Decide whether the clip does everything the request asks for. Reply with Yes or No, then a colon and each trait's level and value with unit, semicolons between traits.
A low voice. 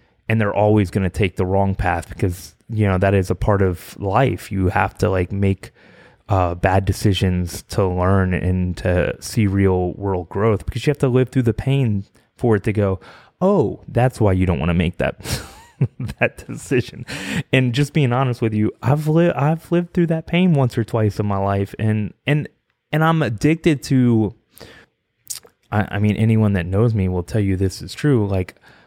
Yes: low, 105 Hz